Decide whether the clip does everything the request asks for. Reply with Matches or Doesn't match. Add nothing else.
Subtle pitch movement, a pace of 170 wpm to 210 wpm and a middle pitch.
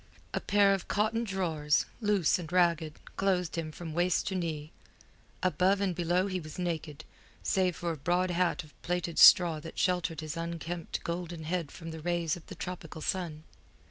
Matches